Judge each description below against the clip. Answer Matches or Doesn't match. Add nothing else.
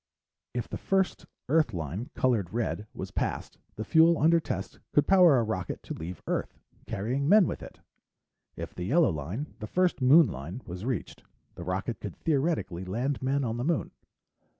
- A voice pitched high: Doesn't match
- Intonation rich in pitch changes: Matches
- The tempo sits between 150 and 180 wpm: Matches